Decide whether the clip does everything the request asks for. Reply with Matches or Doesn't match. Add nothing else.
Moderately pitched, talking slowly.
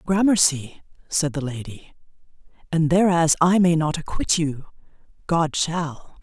Matches